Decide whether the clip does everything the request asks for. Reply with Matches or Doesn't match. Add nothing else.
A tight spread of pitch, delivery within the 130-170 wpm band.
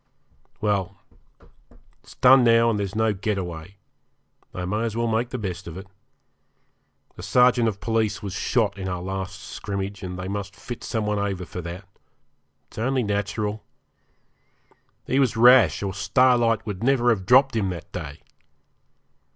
Doesn't match